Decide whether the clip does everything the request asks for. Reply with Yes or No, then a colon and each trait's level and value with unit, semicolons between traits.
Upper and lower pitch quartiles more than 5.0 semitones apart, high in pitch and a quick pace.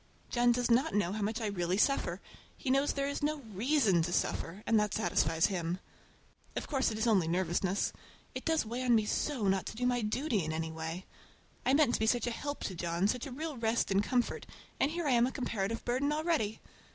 Yes: wide, 5.6 semitones; high, 225 Hz; fast, 225 wpm